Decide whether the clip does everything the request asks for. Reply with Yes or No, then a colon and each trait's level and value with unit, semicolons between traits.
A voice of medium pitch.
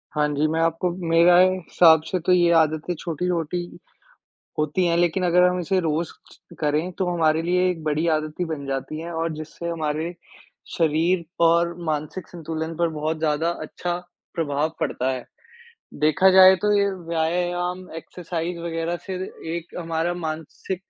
Yes: medium, 165 Hz